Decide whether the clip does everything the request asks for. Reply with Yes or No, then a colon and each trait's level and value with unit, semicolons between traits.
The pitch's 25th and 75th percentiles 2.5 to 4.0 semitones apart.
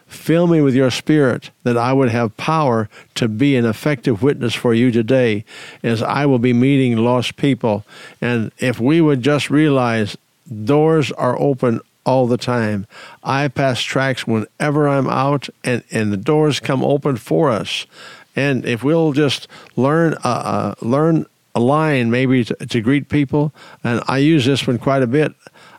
Yes: average, 3.4 semitones